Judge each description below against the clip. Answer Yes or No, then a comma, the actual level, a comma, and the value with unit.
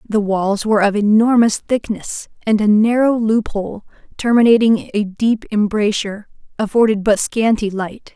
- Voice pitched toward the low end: No, high, 215 Hz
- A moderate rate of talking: No, slow, 130 wpm